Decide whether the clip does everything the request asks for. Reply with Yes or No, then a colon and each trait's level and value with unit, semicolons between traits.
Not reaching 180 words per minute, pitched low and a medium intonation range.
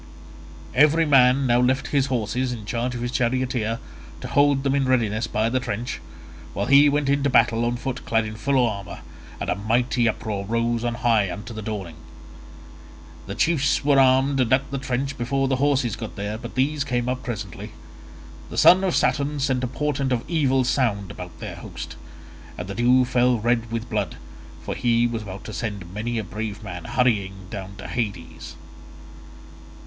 No: average, 185 wpm; low, 120 Hz; average, 3.5 semitones